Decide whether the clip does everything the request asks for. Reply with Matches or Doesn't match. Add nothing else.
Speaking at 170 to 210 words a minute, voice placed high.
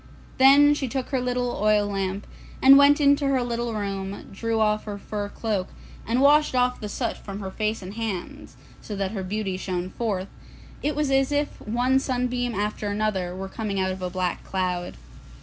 Matches